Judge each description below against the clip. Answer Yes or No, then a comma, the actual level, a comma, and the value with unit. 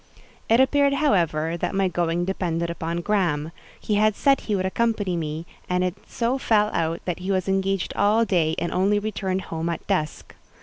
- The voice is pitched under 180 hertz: No, medium, 185 Hz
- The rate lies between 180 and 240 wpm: Yes, average, 185 wpm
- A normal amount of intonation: Yes, average, 3.8 semitones